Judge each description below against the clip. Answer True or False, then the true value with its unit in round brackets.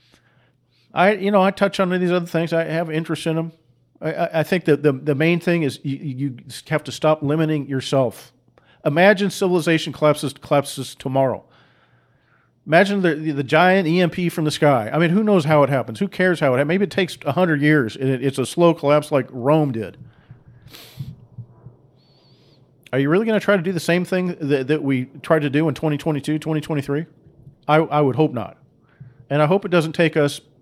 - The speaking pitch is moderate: True (150 Hz)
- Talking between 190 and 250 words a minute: True (205 wpm)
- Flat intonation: False (3.7 semitones)